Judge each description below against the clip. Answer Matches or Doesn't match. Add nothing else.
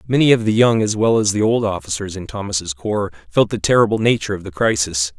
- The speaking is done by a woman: Doesn't match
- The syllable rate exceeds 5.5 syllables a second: Matches